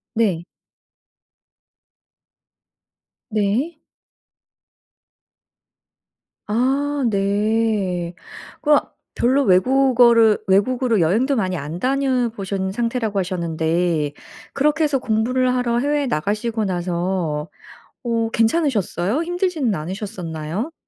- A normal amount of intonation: No, wide, 5.7 semitones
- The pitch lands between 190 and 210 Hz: No, high, 220 Hz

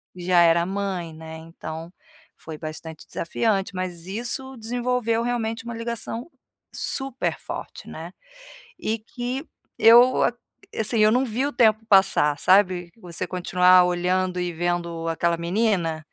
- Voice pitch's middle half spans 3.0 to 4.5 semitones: No, average, 5.1 semitones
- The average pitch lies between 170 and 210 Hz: Yes, medium, 185 Hz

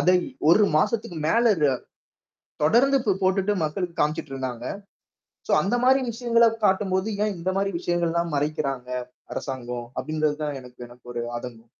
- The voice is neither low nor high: Yes, medium, 170 Hz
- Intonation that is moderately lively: No, wide, 6.9 semitones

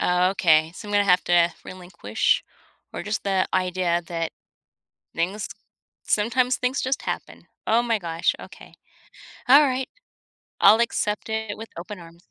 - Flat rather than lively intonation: No, average, 4.2 semitones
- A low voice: No, high, 195 Hz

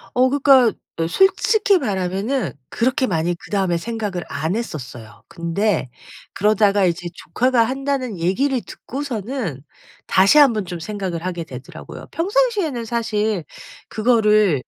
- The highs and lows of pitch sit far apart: Yes, wide, 6.5 semitones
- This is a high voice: Yes, high, 215 Hz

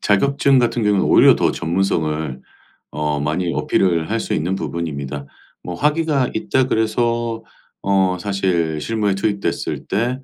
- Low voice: Yes, very low, 95 Hz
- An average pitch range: No, wide, 6.1 semitones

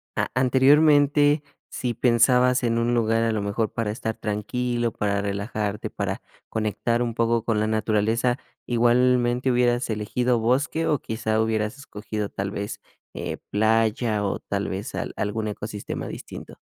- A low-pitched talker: Yes, low, 115 Hz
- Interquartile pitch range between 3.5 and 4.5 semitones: No, average, 2.7 semitones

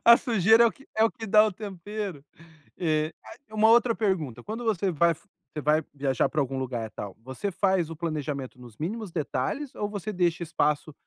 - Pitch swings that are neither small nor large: No, wide, 6.3 semitones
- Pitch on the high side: No, medium, 175 Hz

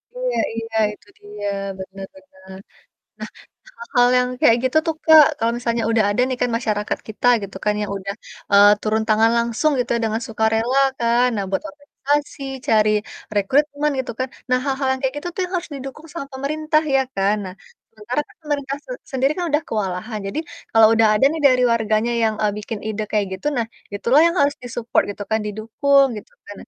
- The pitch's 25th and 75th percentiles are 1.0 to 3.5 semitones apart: No, average, 4.6 semitones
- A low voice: No, high, 235 Hz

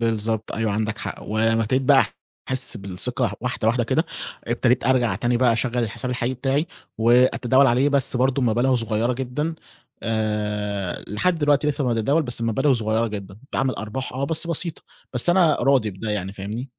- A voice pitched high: No, low, 120 Hz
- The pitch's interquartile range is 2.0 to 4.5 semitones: Yes, average, 3.2 semitones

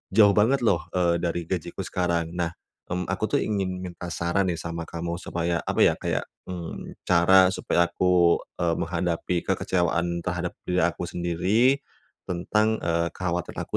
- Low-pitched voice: Yes, very low, 85 Hz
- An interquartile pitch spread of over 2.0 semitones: No, narrow, 1.4 semitones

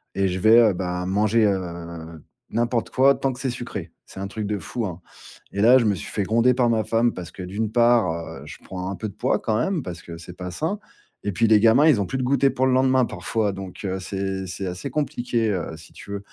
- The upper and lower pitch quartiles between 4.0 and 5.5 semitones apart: Yes, average, 4.4 semitones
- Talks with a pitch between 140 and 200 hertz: No, low, 105 Hz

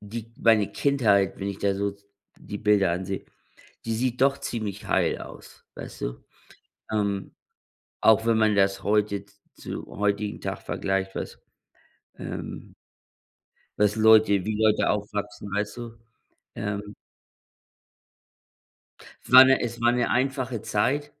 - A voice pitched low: Yes, low, 105 Hz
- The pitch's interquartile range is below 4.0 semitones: Yes, narrow, 2.4 semitones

